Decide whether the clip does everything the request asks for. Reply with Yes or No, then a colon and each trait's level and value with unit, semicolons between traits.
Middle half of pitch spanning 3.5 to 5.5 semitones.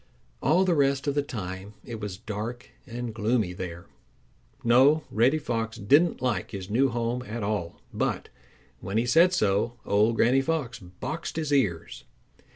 Yes: average, 4.8 semitones